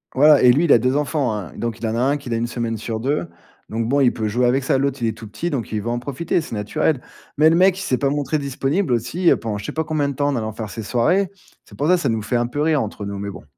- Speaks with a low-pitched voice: Yes, low, 125 Hz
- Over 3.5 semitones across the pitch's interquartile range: Yes, average, 4.5 semitones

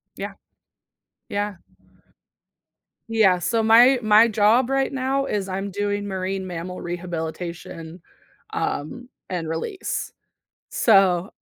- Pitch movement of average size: Yes, average, 4.1 semitones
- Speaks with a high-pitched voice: Yes, high, 200 Hz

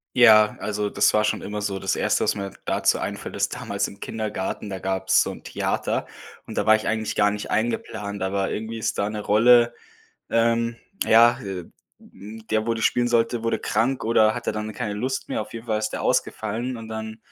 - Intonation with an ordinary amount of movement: No, narrow, 2.0 semitones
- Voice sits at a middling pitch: No, low, 110 Hz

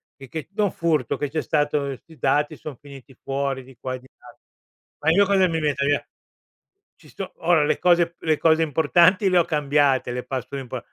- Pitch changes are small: No, average, 3.3 semitones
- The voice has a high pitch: No, medium, 150 Hz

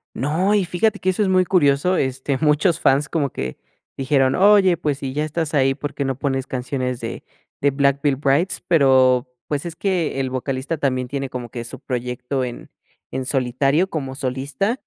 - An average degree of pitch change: Yes, average, 3.8 semitones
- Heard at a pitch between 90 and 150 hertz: Yes, medium, 140 Hz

